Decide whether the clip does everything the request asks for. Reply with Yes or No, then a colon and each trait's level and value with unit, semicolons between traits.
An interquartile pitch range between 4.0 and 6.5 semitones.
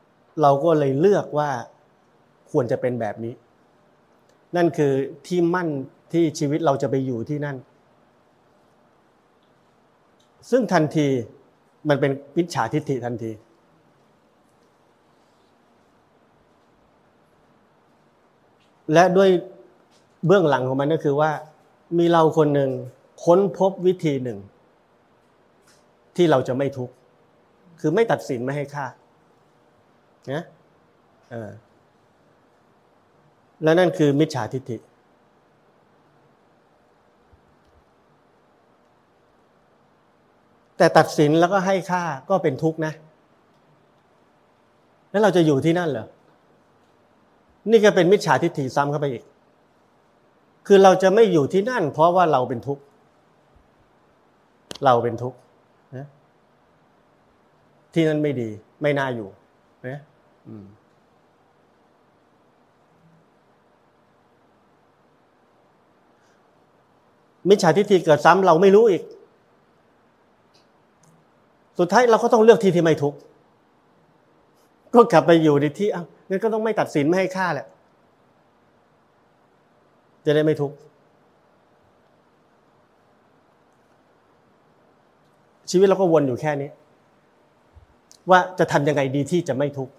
Yes: average, 4.7 semitones